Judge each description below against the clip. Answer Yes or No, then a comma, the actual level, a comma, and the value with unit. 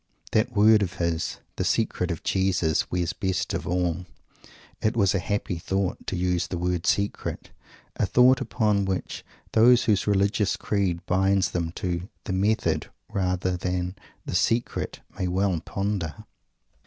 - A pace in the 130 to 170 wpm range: Yes, average, 150 wpm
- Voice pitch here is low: Yes, very low, 95 Hz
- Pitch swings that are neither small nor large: No, narrow, 2.3 semitones